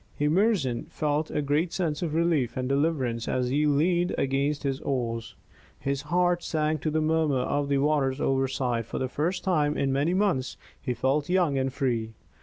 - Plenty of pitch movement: No, average, 3.2 semitones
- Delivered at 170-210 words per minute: Yes, average, 180 wpm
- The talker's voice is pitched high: No, medium, 145 Hz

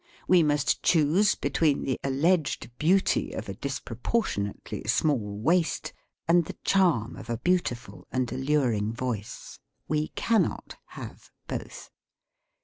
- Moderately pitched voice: Yes, medium, 145 Hz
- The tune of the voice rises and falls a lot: Yes, wide, 6.1 semitones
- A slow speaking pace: Yes, slow, 130 wpm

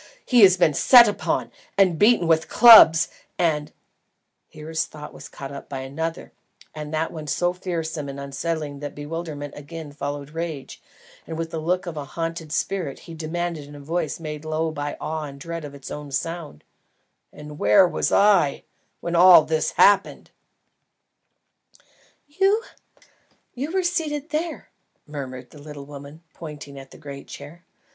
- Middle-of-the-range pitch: Yes, medium, 160 Hz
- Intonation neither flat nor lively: Yes, average, 3.1 semitones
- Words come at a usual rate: Yes, average, 160 wpm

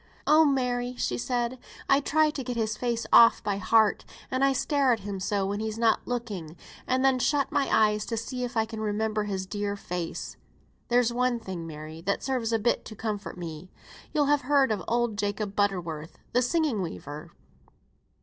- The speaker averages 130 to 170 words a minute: No, average, 190 wpm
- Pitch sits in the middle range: No, high, 225 Hz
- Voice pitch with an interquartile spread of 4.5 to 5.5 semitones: No, average, 3.9 semitones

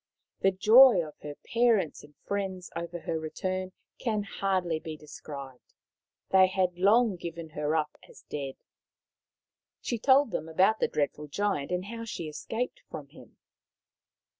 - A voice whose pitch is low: No, medium, 185 Hz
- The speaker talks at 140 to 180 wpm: Yes, average, 145 wpm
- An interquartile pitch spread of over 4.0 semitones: Yes, average, 4.8 semitones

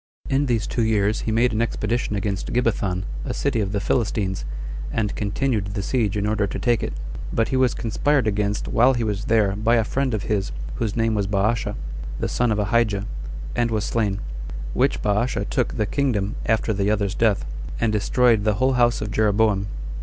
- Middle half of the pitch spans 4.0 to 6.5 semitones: No, narrow, 2.5 semitones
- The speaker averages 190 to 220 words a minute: Yes, average, 195 wpm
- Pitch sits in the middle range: No, low, 110 Hz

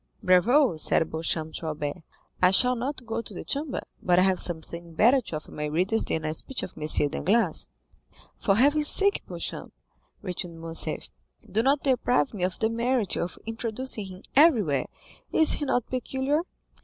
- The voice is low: No, high, 210 Hz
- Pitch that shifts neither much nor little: No, wide, 7.4 semitones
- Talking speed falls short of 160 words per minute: No, average, 170 wpm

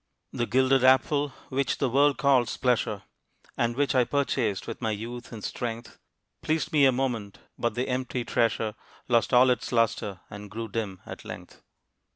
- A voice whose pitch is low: Yes, low, 120 Hz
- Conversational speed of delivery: Yes, average, 170 wpm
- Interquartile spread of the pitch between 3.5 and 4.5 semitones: No, average, 2.7 semitones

